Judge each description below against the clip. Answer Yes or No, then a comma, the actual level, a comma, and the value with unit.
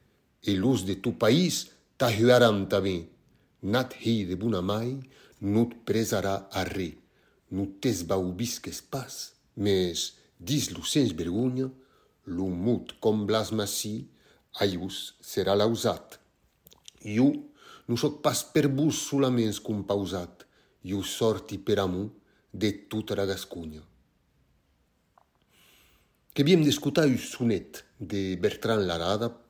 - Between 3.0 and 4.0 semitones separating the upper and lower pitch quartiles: Yes, average, 3.6 semitones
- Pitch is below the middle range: Yes, low, 105 Hz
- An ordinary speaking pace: No, slow, 100 wpm